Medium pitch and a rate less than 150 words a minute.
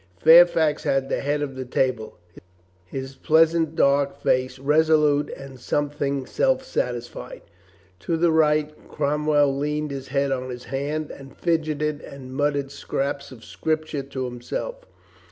Yes: medium, 145 Hz; average, 140 wpm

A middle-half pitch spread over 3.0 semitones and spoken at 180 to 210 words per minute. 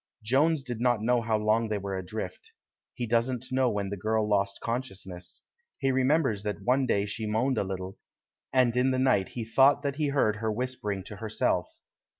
Yes: average, 3.9 semitones; average, 185 wpm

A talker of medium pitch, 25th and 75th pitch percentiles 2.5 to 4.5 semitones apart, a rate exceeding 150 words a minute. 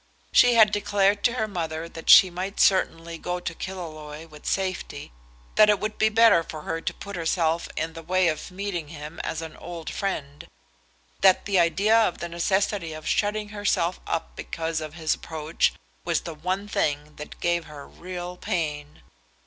Yes: medium, 170 Hz; average, 3.7 semitones; average, 180 wpm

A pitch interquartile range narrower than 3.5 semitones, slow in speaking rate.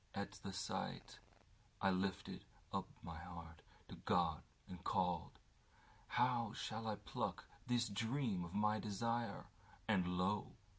No: average, 3.8 semitones; slow, 110 wpm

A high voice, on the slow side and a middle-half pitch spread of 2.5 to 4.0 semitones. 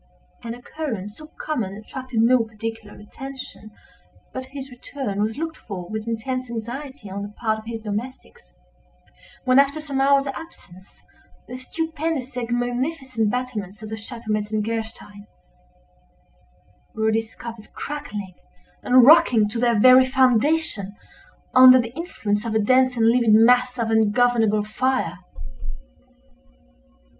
Yes: high, 235 Hz; slow, 130 wpm; average, 3.2 semitones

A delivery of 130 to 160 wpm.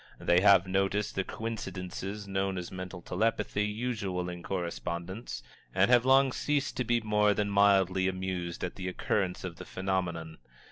Yes: average, 155 wpm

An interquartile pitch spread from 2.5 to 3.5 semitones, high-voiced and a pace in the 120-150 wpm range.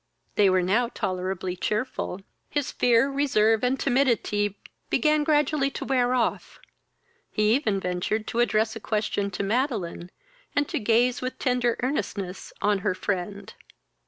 No: average, 4.4 semitones; high, 225 Hz; average, 140 wpm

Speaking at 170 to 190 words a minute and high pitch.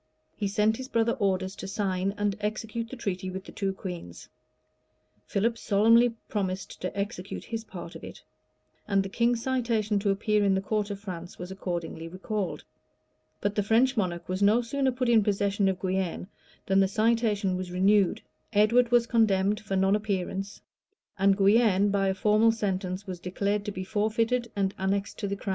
Yes: average, 185 wpm; high, 200 Hz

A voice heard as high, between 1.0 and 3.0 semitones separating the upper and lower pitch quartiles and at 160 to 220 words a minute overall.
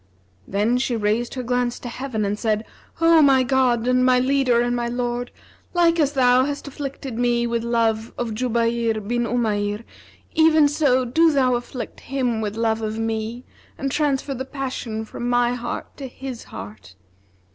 Yes: high, 245 Hz; average, 2.7 semitones; average, 170 wpm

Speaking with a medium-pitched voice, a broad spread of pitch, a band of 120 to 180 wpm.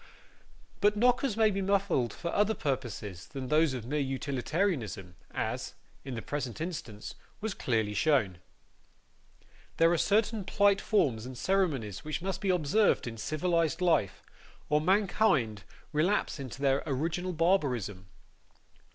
Yes: medium, 155 Hz; wide, 7.5 semitones; slow, 135 wpm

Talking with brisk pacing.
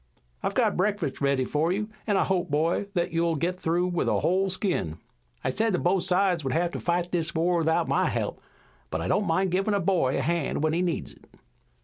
Yes: fast, 230 wpm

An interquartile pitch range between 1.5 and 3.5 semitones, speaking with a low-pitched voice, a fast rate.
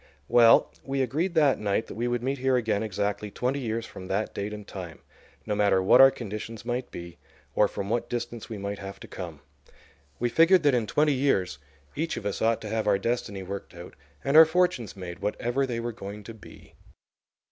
No: average, 4.2 semitones; low, 115 Hz; fast, 210 wpm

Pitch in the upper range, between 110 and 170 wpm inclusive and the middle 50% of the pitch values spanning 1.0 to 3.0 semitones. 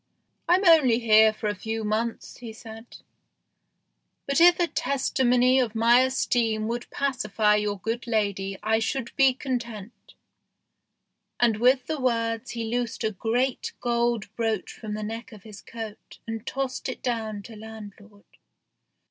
Yes: high, 230 Hz; average, 150 wpm; narrow, 2.5 semitones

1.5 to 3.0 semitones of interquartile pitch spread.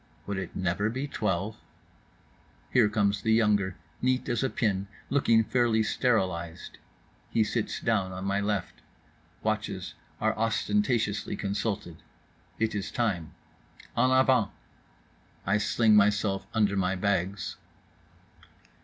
Yes: narrow, 2.6 semitones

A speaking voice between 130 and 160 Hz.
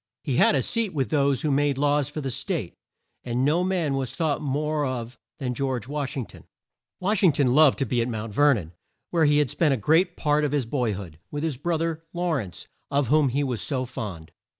Yes: medium, 140 Hz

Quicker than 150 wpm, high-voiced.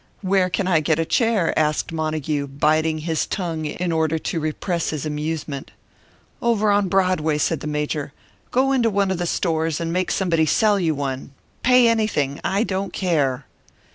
No: average, 170 wpm; medium, 165 Hz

